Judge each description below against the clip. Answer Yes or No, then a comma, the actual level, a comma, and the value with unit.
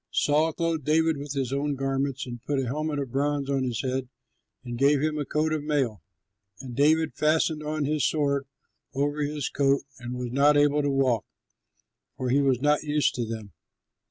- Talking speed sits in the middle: Yes, average, 190 wpm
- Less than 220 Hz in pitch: Yes, medium, 140 Hz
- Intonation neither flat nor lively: No, narrow, 2.2 semitones